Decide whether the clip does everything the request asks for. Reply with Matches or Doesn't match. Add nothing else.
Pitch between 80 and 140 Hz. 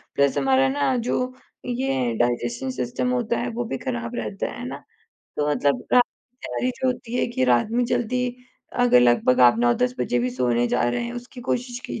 Matches